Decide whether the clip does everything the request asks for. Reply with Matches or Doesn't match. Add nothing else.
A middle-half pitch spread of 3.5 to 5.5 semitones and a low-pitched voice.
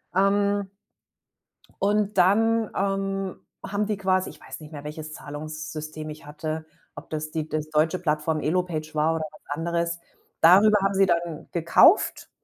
Doesn't match